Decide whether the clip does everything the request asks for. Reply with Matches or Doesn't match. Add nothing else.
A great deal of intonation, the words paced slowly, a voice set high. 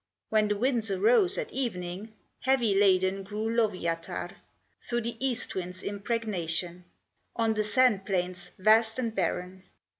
Doesn't match